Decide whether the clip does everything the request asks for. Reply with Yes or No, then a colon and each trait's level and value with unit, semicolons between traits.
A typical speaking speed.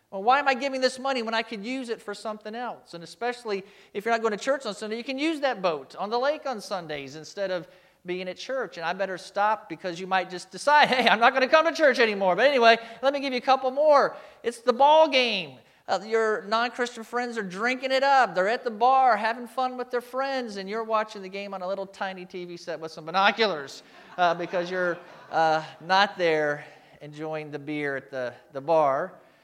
No: fast, 235 wpm